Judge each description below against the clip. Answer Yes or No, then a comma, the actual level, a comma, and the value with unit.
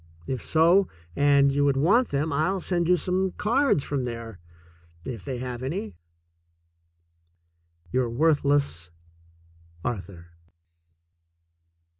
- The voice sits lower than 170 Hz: Yes, medium, 140 Hz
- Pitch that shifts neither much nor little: No, wide, 6.2 semitones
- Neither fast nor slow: No, slow, 110 wpm